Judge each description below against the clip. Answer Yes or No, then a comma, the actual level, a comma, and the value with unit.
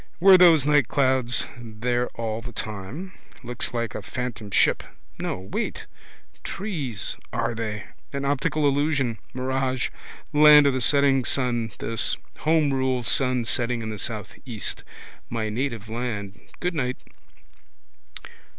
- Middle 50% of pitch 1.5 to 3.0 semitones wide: No, average, 3.7 semitones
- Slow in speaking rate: Yes, slow, 120 wpm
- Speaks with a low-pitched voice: Yes, low, 125 Hz